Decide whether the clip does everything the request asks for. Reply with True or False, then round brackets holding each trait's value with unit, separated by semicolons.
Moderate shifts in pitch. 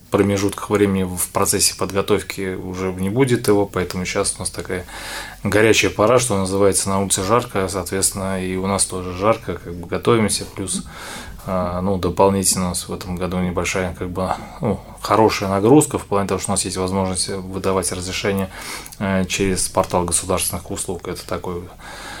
False (1.4 semitones)